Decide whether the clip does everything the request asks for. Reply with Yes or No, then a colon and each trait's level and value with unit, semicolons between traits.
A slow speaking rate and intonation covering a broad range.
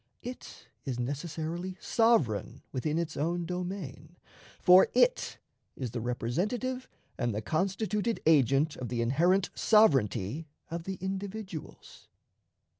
Yes: slow, 115 wpm; wide, 6.4 semitones